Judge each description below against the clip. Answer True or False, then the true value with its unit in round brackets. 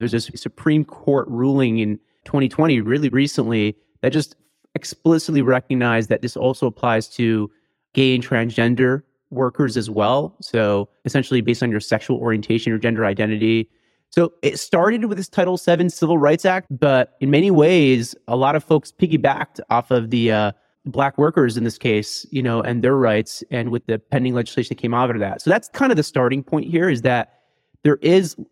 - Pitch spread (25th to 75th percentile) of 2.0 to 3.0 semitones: False (4.3 semitones)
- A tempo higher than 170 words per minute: True (185 wpm)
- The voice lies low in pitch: True (130 Hz)